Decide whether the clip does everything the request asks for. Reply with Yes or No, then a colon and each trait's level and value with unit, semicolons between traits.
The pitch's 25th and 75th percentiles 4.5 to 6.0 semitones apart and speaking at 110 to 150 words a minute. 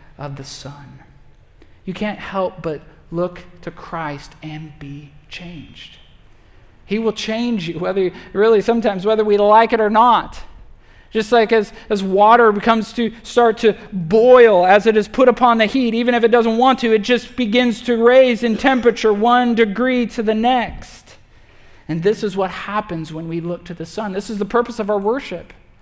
No: average, 5.0 semitones; average, 185 wpm